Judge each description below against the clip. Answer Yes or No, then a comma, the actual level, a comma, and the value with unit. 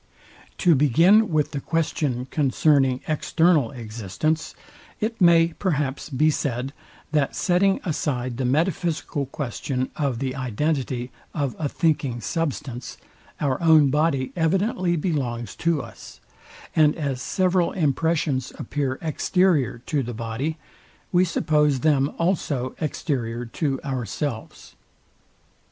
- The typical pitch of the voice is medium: Yes, medium, 145 Hz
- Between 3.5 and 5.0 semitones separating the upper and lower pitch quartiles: Yes, average, 4.1 semitones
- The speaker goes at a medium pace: No, slow, 115 wpm